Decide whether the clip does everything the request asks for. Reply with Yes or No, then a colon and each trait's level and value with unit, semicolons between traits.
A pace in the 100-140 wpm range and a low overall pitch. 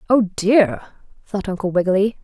No: slow, 135 wpm; high, 200 Hz